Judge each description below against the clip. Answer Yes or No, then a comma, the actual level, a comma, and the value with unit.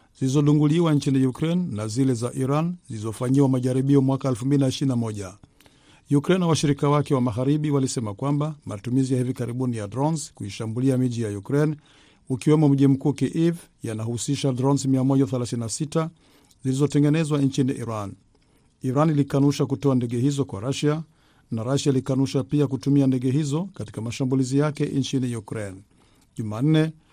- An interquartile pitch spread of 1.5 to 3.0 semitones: Yes, narrow, 2.6 semitones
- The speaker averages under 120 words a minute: No, average, 135 wpm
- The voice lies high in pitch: No, low, 135 Hz